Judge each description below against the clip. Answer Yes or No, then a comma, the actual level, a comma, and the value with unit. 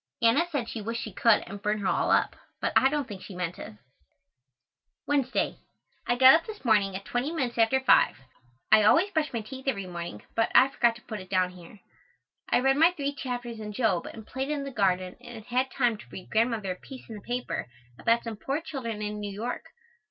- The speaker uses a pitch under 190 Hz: No, high, 230 Hz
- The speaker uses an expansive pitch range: No, average, 4.3 semitones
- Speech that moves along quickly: Yes, fast, 220 wpm